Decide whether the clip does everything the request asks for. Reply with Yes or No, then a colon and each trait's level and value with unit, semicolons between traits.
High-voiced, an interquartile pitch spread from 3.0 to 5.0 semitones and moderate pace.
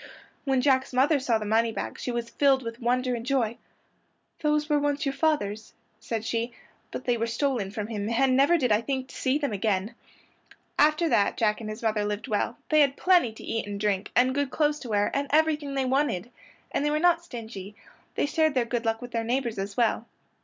No: high, 245 Hz; average, 4.2 semitones; fast, 215 wpm